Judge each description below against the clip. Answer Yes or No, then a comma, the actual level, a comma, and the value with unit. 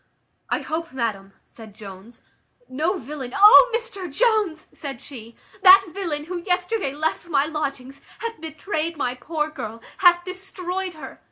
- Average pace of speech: Yes, average, 145 wpm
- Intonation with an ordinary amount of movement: No, wide, 5.7 semitones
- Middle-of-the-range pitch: No, very high, 315 Hz